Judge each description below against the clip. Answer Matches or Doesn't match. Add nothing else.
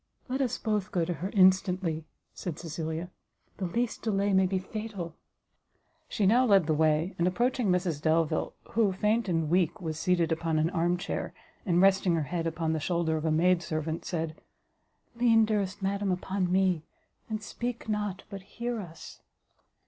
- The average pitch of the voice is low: Doesn't match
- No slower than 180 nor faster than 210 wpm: Doesn't match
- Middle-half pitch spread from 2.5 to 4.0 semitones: Matches